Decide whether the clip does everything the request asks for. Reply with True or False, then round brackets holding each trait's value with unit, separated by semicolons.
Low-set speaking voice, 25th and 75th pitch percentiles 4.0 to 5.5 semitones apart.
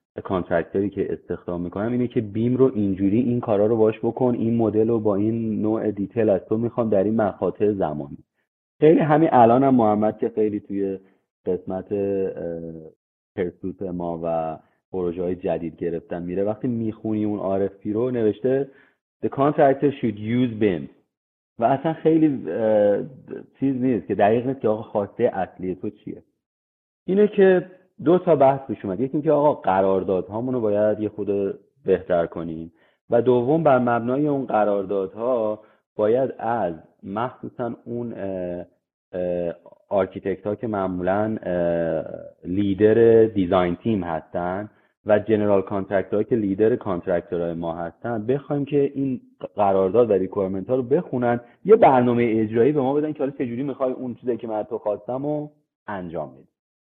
True (110 Hz; 4.8 semitones)